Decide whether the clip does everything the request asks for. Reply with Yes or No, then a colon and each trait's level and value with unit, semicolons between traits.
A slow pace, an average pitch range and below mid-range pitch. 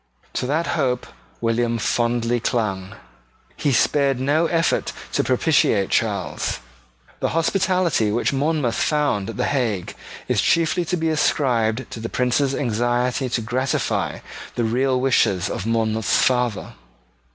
Yes: slow, 130 wpm; average, 4.0 semitones; low, 125 Hz